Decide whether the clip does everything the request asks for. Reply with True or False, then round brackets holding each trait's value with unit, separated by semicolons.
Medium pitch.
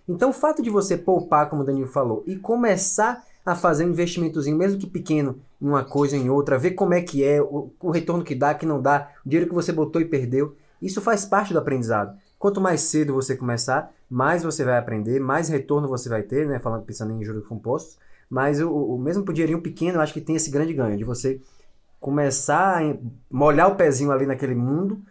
True (145 Hz)